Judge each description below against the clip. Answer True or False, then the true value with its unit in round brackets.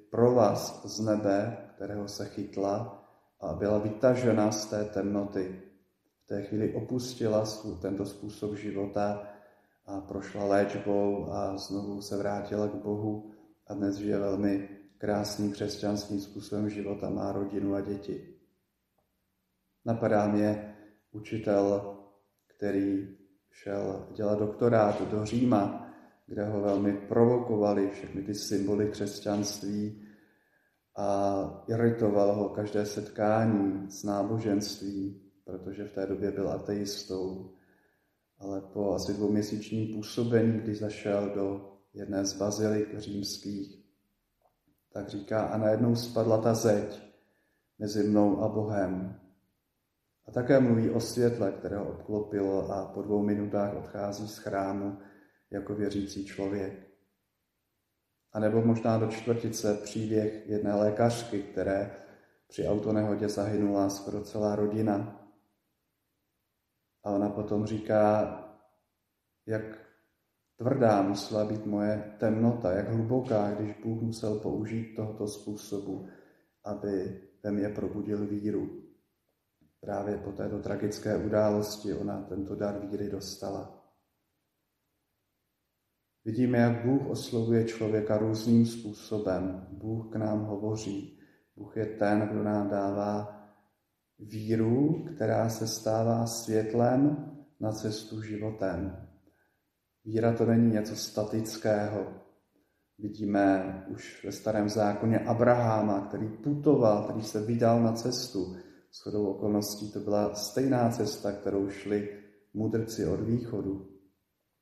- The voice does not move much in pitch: True (1.4 semitones)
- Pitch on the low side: True (105 Hz)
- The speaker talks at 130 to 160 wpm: False (115 wpm)